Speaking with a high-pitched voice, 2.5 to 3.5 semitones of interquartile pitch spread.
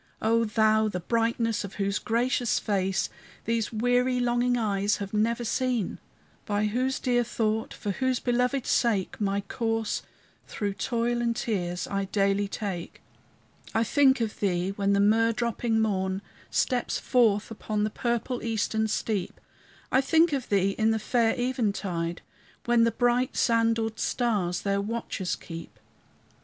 Yes: high, 220 Hz; average, 3.1 semitones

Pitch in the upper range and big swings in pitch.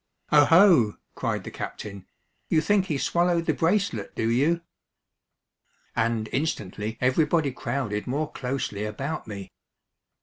No: medium, 140 Hz; wide, 6.7 semitones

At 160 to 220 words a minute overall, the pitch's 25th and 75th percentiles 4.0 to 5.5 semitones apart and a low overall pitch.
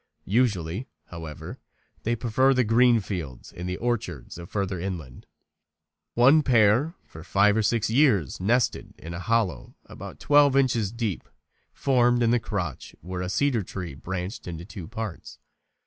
No: average, 150 wpm; average, 5.2 semitones; low, 105 Hz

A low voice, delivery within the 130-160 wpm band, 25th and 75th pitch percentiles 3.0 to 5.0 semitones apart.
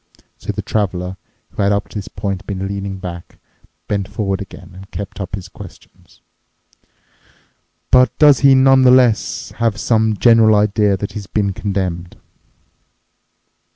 No: low, 100 Hz; average, 140 wpm; narrow, 2.4 semitones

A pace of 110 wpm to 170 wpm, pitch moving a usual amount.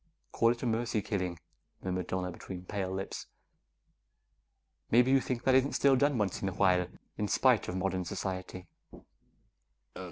Yes: average, 155 wpm; average, 4.6 semitones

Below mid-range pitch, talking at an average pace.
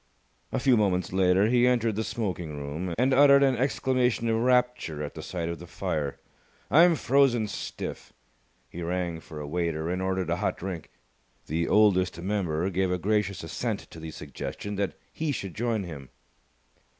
Yes: very low, 95 Hz; average, 175 wpm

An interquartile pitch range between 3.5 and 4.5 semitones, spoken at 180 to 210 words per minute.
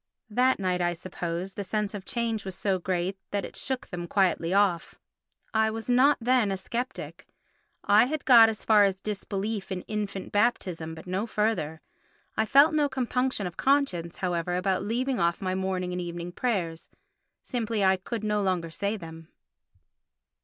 No: average, 3.9 semitones; average, 165 wpm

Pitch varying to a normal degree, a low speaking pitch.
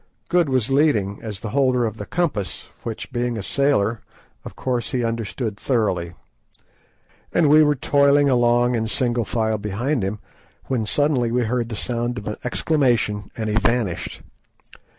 Yes: average, 3.6 semitones; low, 120 Hz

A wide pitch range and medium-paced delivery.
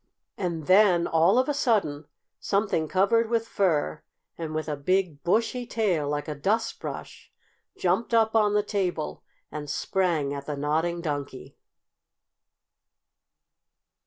No: wide, 5.7 semitones; slow, 130 wpm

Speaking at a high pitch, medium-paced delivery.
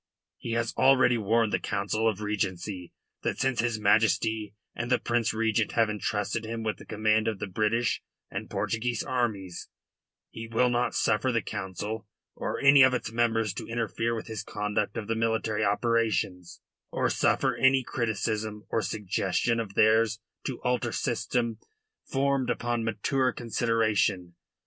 No: low, 110 Hz; average, 155 wpm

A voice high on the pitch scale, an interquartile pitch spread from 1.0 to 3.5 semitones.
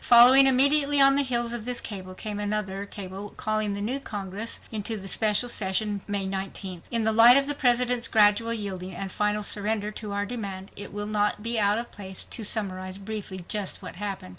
Yes: high, 210 Hz; average, 3.0 semitones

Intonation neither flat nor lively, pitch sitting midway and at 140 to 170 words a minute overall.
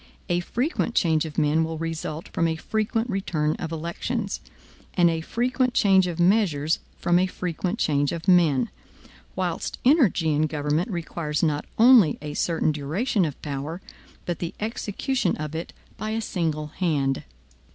Yes: average, 4.4 semitones; medium, 170 Hz; average, 155 wpm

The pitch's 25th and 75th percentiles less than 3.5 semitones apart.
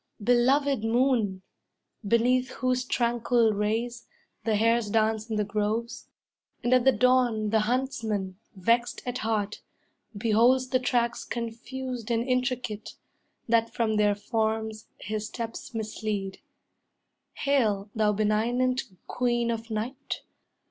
Yes: narrow, 2.6 semitones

